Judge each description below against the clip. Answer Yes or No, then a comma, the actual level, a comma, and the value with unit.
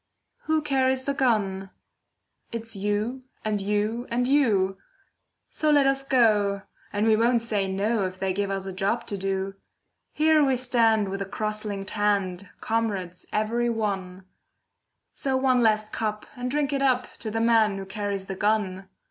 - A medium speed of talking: Yes, average, 165 wpm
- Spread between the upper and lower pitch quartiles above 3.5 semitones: Yes, average, 4.0 semitones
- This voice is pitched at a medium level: No, high, 215 Hz